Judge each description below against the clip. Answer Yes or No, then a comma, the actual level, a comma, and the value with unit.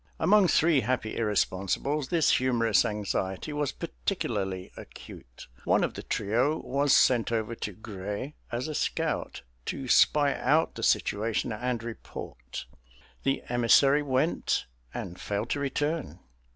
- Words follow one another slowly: Yes, slow, 130 wpm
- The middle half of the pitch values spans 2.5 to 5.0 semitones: No, wide, 5.5 semitones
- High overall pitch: No, low, 120 Hz